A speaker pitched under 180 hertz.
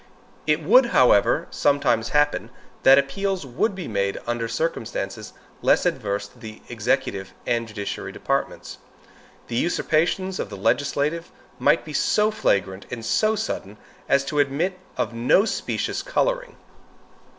Yes: medium, 140 Hz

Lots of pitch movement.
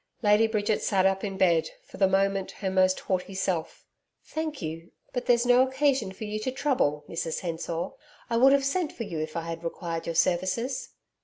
Yes: wide, 6.1 semitones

